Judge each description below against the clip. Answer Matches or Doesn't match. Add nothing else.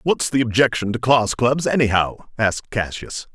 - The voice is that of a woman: Doesn't match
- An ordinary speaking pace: Matches